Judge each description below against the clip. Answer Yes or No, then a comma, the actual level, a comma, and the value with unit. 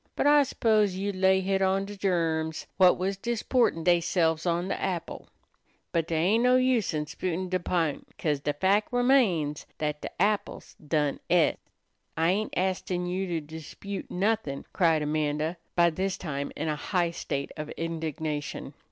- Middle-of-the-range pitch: Yes, medium, 175 Hz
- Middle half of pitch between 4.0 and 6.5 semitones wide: No, average, 3.6 semitones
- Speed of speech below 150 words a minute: No, average, 165 wpm